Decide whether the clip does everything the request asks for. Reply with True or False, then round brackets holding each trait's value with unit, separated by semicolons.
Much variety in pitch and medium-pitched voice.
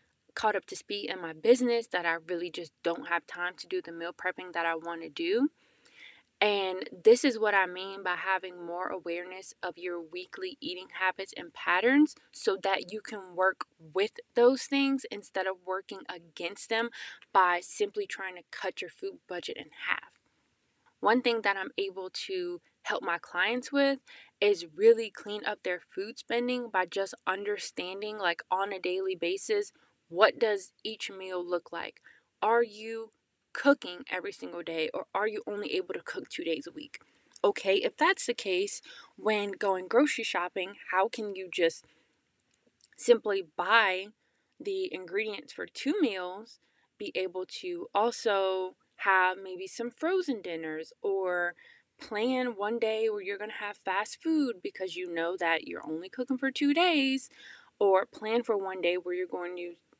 False (6.9 semitones; 205 Hz)